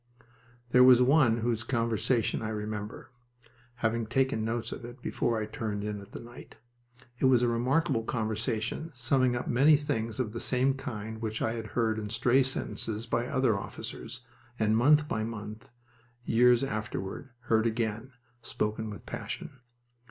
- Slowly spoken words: No, average, 155 wpm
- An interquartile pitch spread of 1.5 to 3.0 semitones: Yes, narrow, 2.4 semitones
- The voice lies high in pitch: No, low, 115 Hz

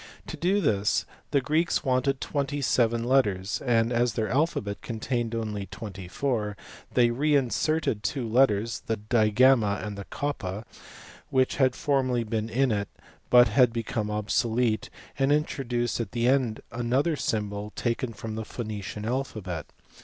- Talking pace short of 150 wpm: Yes, average, 140 wpm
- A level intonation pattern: No, average, 3.7 semitones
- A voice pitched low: Yes, low, 115 Hz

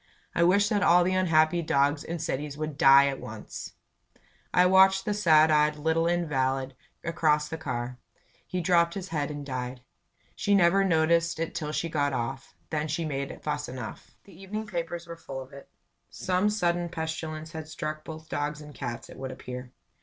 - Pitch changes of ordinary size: Yes, average, 3.3 semitones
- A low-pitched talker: No, medium, 160 Hz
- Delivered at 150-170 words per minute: No, average, 185 wpm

